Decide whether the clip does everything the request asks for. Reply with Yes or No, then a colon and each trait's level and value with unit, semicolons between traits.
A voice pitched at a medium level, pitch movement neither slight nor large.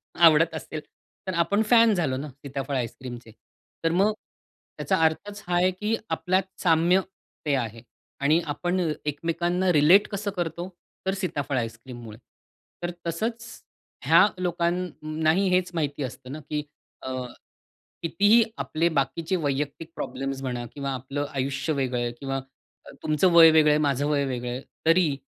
Yes: medium, 155 Hz; average, 4.6 semitones